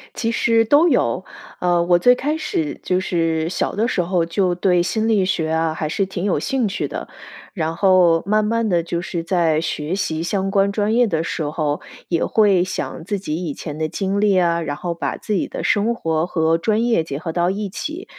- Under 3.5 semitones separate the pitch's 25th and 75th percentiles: No, average, 4.0 semitones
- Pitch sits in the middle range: Yes, medium, 180 Hz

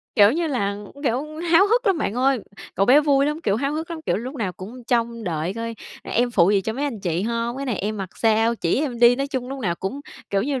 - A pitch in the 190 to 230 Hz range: No, high, 240 Hz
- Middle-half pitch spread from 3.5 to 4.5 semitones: No, average, 5.2 semitones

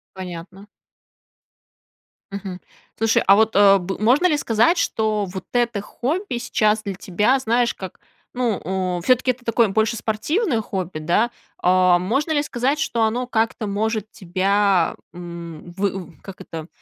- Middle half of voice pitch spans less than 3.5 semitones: No, average, 4.2 semitones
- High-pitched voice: Yes, high, 215 Hz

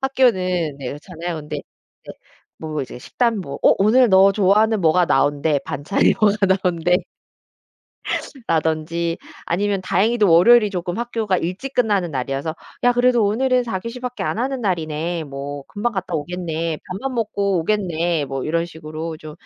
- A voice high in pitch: No, medium, 180 Hz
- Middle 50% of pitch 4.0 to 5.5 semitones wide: Yes, average, 5.1 semitones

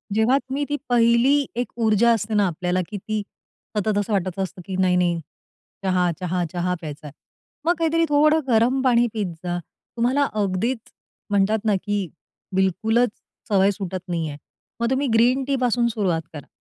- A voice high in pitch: Yes, high, 210 Hz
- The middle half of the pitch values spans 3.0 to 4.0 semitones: No, average, 4.7 semitones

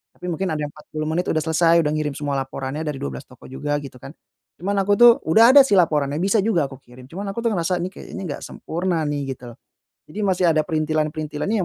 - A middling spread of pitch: Yes, average, 4.3 semitones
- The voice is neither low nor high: Yes, medium, 155 Hz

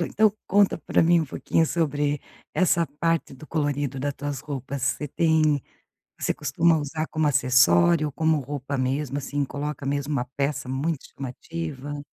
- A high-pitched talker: No, medium, 145 Hz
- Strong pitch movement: No, narrow, 2.6 semitones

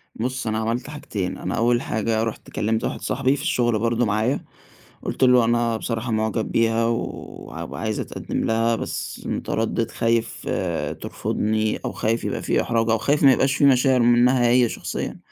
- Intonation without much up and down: Yes, narrow, 1.8 semitones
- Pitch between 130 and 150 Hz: No, low, 115 Hz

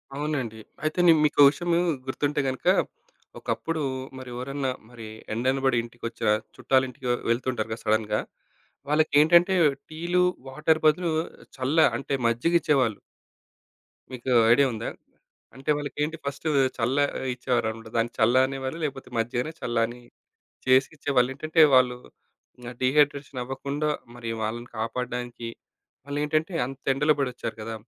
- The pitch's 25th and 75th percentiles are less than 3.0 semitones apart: No, average, 3.6 semitones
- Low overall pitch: Yes, low, 130 Hz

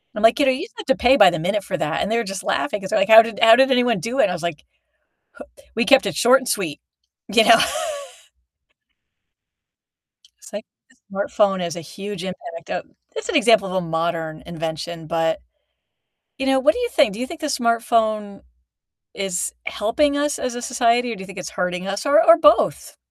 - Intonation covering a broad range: Yes, wide, 6.0 semitones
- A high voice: Yes, high, 220 Hz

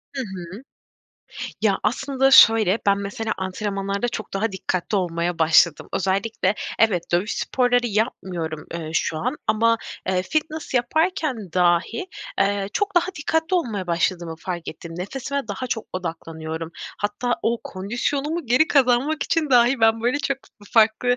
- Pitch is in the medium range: No, high, 215 Hz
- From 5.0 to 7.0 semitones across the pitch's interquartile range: Yes, wide, 5.6 semitones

